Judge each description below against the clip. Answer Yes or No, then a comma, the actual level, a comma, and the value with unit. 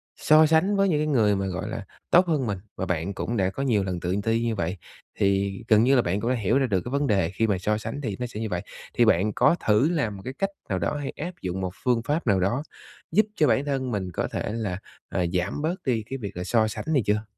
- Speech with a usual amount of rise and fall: No, wide, 6.0 semitones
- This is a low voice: Yes, low, 110 Hz